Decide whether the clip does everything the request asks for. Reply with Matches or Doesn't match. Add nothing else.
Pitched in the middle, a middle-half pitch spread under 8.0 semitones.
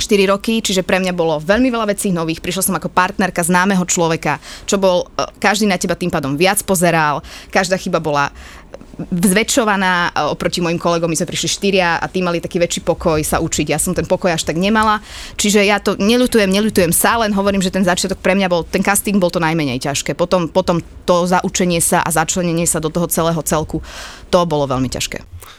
Matches